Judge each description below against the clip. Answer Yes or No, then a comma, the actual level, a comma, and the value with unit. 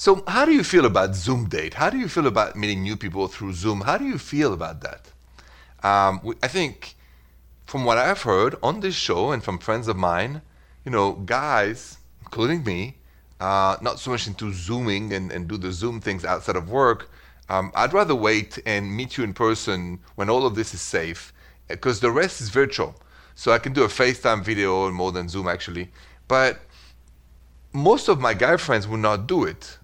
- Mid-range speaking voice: No, low, 100 Hz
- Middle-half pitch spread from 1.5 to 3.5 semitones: No, average, 4.7 semitones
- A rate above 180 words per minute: Yes, fast, 205 wpm